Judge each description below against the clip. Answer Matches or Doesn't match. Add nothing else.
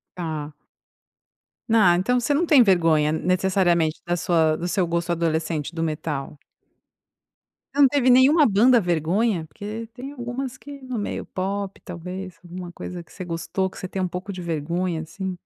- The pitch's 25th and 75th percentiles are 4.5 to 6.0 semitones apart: Matches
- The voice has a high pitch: Doesn't match